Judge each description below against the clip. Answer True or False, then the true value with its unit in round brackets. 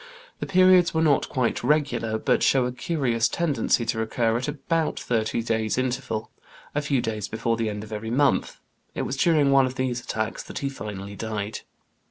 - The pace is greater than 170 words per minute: True (190 wpm)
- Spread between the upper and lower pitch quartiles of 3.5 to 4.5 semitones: True (4.1 semitones)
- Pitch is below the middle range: True (125 Hz)